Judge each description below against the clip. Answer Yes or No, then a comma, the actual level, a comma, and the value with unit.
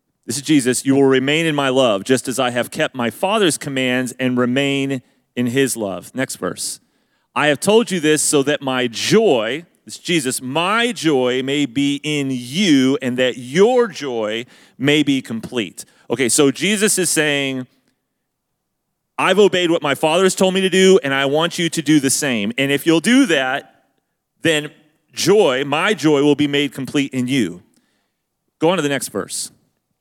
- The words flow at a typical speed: Yes, average, 185 wpm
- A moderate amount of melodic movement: Yes, average, 4.0 semitones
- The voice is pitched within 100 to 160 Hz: Yes, medium, 140 Hz